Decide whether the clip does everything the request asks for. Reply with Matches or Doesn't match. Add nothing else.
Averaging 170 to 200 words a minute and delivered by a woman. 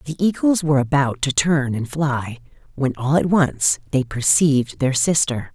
Matches